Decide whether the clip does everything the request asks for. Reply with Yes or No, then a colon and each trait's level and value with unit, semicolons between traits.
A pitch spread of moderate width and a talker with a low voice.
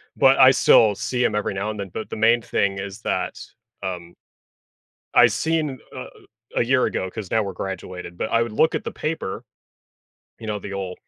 Yes: average, 4.2 semitones; low, 105 Hz